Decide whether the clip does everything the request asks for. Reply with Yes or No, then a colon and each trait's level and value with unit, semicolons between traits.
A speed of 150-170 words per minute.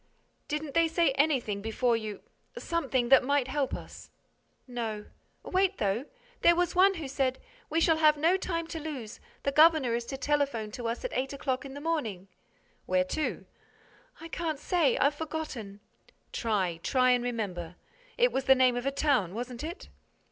Yes: average, 160 wpm